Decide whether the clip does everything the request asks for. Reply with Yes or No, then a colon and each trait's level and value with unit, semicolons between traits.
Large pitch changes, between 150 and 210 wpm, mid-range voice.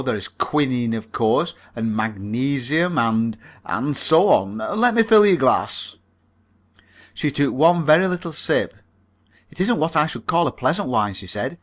Yes: wide, 7.3 semitones; average, 170 wpm; medium, 145 Hz